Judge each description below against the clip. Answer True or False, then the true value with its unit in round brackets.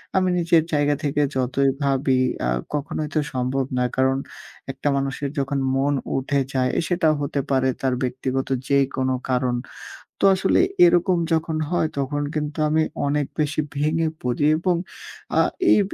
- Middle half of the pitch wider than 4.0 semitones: False (2.9 semitones)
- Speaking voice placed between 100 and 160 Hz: True (140 Hz)